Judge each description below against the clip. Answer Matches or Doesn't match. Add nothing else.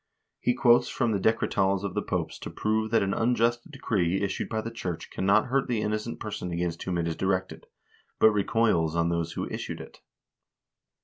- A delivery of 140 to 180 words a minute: Doesn't match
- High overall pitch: Doesn't match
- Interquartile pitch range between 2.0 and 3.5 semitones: Doesn't match